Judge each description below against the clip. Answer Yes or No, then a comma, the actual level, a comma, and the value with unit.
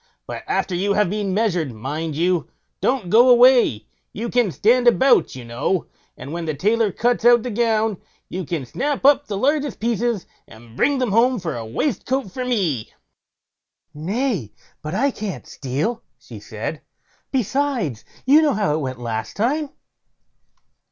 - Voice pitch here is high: Yes, high, 210 Hz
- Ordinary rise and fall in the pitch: No, wide, 7.8 semitones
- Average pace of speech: Yes, average, 160 wpm